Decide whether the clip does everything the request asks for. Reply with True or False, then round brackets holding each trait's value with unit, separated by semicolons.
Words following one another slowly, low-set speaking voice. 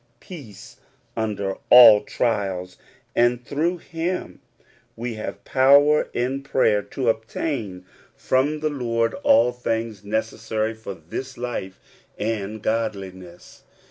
True (110 wpm; 115 Hz)